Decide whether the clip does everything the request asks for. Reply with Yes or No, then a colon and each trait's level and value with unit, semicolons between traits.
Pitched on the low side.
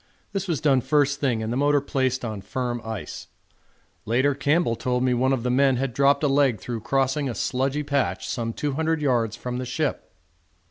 Yes: low, 130 Hz